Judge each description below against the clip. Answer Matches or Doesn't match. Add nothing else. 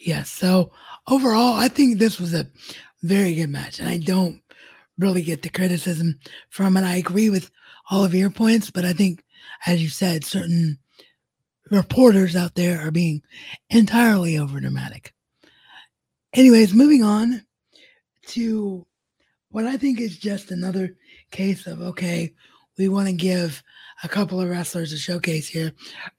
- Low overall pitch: Doesn't match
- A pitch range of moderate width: Matches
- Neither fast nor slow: Matches